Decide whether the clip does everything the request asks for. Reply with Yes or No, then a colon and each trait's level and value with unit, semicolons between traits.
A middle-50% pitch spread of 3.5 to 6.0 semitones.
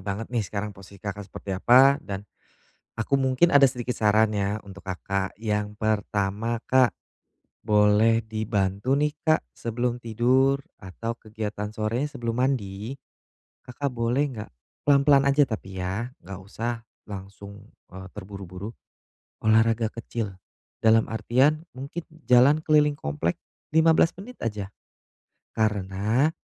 Yes: average, 4.2 semitones